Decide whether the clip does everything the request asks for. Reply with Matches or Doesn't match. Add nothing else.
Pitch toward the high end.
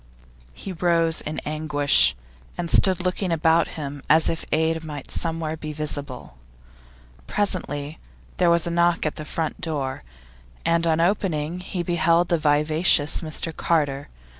Doesn't match